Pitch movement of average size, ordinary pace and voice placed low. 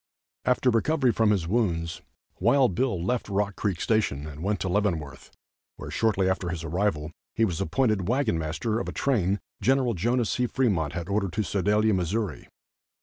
Yes: average, 4.9 semitones; average, 170 wpm; low, 100 Hz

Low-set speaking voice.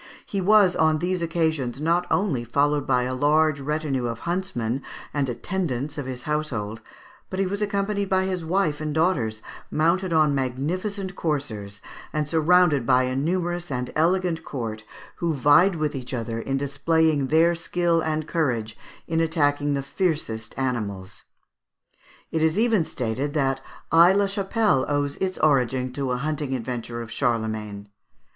No: medium, 150 Hz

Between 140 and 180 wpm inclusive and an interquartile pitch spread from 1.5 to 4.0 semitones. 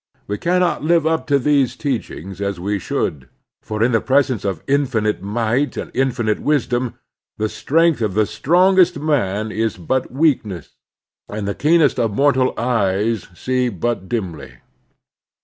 No: average, 150 wpm; wide, 5.6 semitones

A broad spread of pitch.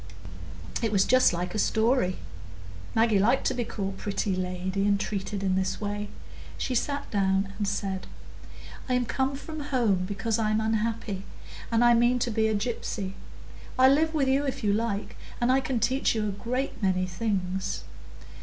No: average, 4.0 semitones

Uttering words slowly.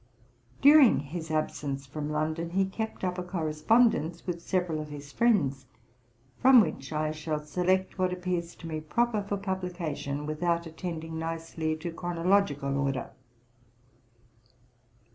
Yes: slow, 130 wpm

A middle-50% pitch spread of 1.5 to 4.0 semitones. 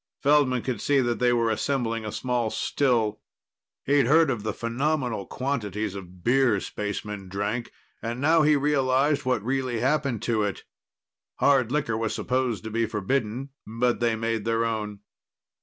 Yes: average, 3.5 semitones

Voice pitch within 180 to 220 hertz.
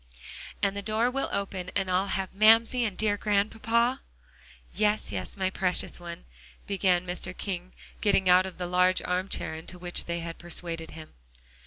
Yes: medium, 185 Hz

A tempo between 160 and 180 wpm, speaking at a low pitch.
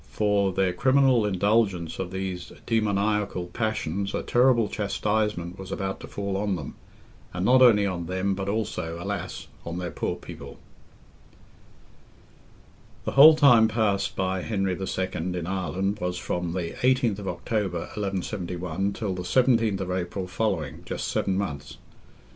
No: average, 140 wpm; very low, 95 Hz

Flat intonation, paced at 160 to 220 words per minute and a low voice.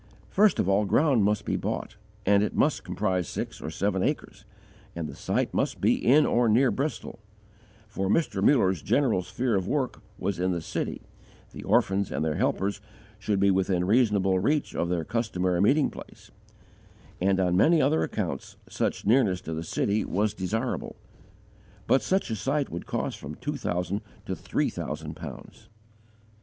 No: average, 5.0 semitones; average, 170 wpm; low, 100 Hz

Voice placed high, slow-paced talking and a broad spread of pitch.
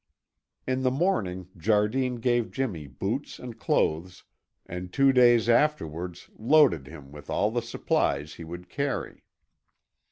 No: low, 105 Hz; slow, 130 wpm; wide, 7.2 semitones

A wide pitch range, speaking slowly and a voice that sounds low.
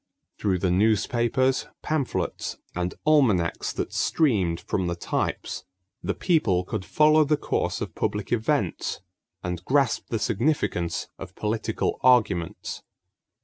Yes: wide, 7.0 semitones; slow, 120 wpm; low, 110 Hz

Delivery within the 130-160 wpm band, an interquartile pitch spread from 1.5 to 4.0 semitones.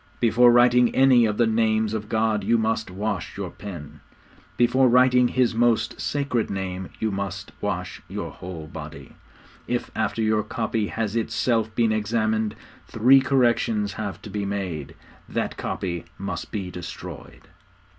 Yes: average, 145 wpm; average, 2.9 semitones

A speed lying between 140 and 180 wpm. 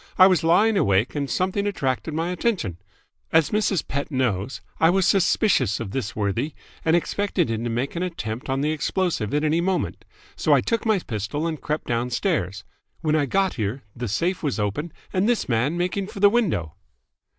No: average, 190 wpm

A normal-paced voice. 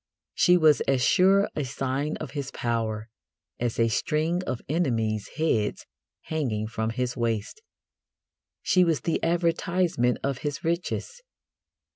No: slow, 130 wpm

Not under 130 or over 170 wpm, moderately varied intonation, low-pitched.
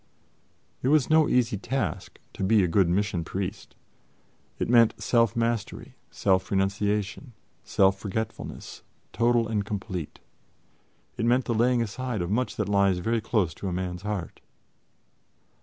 Yes: average, 140 wpm; average, 3.5 semitones; low, 105 Hz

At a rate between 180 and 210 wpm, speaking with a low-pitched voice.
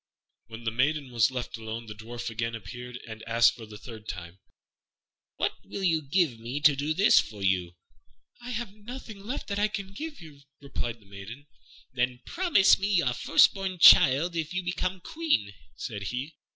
Yes: average, 185 wpm; low, 130 Hz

